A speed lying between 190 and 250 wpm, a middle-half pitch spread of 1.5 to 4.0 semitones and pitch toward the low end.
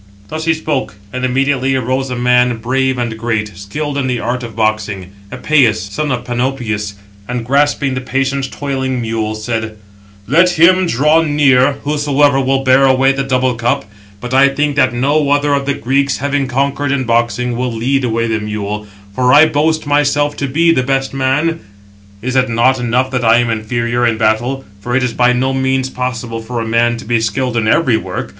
Yes: average, 195 wpm; average, 2.9 semitones; low, 130 Hz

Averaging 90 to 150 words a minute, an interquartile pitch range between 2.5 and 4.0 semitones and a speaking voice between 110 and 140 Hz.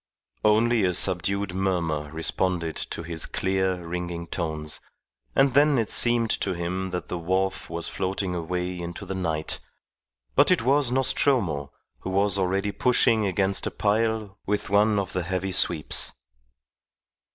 No: average, 145 wpm; average, 3.3 semitones; very low, 95 Hz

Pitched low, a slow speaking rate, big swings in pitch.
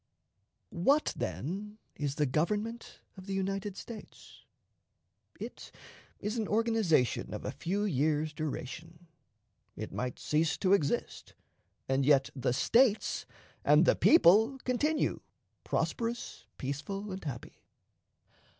No: medium, 185 Hz; slow, 115 wpm; wide, 6.5 semitones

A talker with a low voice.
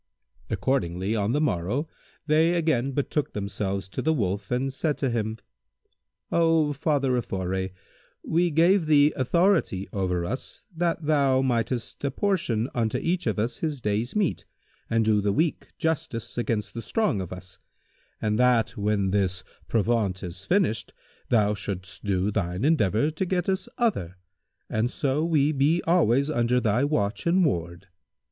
Yes: low, 120 Hz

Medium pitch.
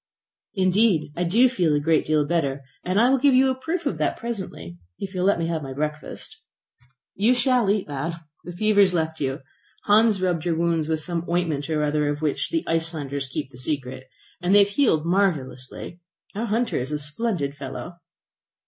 Yes: medium, 170 Hz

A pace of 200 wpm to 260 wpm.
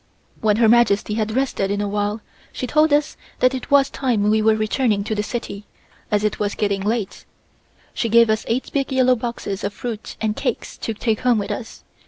Yes: fast, 205 wpm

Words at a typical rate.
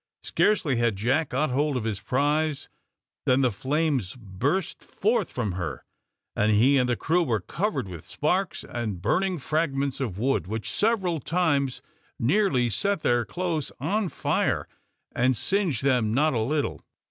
Yes: average, 155 wpm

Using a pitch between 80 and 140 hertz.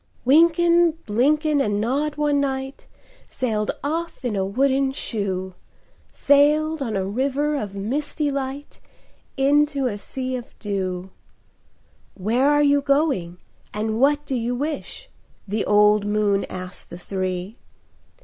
No: very high, 265 Hz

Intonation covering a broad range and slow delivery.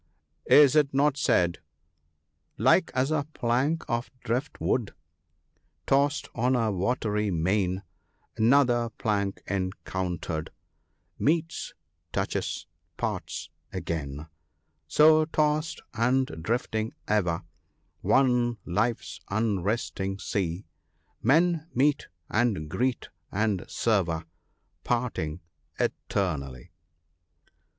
Yes: wide, 6.2 semitones; slow, 95 wpm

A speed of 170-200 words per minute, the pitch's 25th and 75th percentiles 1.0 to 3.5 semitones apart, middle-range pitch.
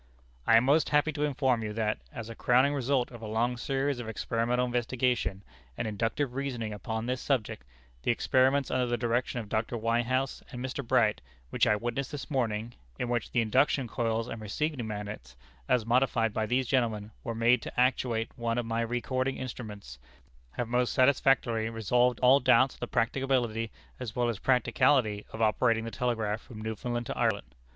No: average, 180 wpm; narrow, 2.4 semitones; low, 120 Hz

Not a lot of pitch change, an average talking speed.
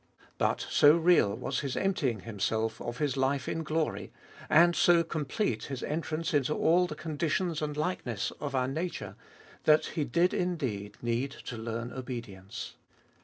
No: wide, 5.5 semitones; average, 160 wpm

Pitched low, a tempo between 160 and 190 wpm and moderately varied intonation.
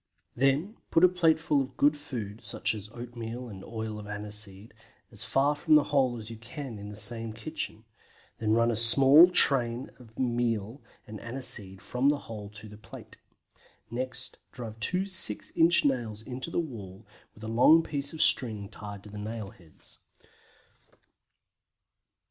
Yes: low, 115 Hz; average, 165 wpm; average, 4.4 semitones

